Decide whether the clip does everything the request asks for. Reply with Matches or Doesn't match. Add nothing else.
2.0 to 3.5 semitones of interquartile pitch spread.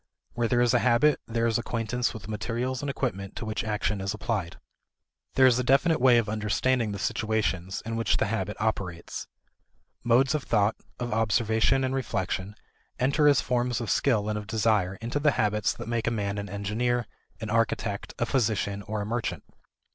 Matches